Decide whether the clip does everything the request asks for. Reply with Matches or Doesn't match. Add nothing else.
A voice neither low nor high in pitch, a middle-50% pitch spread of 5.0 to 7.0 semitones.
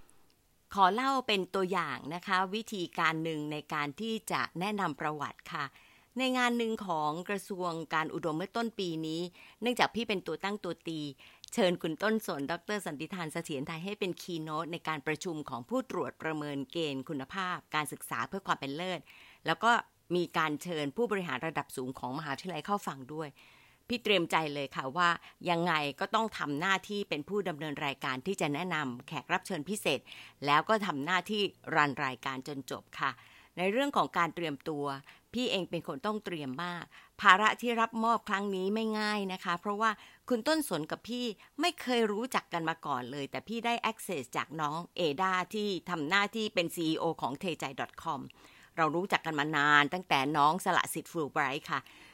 Matches